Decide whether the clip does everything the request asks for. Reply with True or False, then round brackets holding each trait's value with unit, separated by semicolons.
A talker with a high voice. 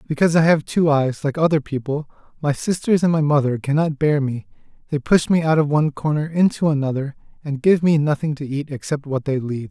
False (145 Hz)